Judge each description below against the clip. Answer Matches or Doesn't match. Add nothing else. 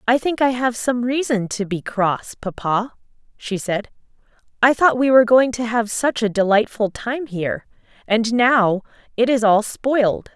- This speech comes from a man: Doesn't match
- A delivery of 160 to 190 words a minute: Matches